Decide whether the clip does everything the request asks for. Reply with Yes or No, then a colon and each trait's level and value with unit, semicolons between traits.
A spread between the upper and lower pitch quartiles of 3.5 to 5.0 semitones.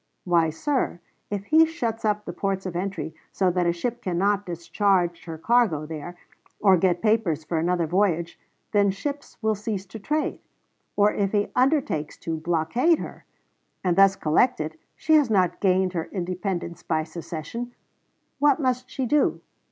Yes: average, 4.7 semitones